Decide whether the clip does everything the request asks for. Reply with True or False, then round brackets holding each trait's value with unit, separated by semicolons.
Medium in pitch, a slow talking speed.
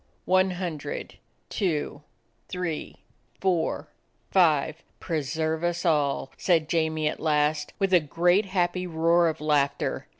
True (165 Hz; 125 wpm)